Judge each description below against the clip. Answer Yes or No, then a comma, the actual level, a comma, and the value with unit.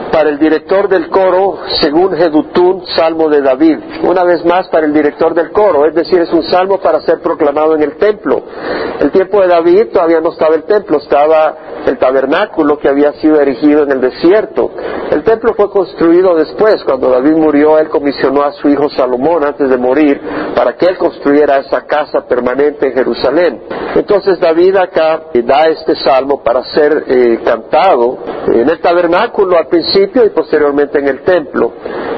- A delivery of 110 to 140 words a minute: No, average, 175 wpm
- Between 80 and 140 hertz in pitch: No, medium, 165 Hz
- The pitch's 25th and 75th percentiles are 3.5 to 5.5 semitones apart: Yes, average, 4.4 semitones